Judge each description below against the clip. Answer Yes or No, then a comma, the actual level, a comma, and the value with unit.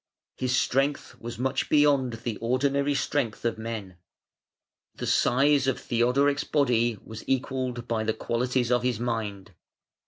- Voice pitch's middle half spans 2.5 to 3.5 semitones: Yes, average, 2.8 semitones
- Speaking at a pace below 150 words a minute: Yes, slow, 135 wpm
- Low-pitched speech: Yes, low, 125 Hz